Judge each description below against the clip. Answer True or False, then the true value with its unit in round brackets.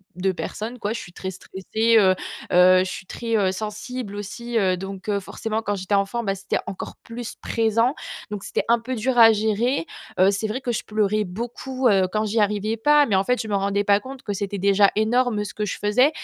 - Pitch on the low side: False (210 Hz)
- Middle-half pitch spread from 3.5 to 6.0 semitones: False (2.8 semitones)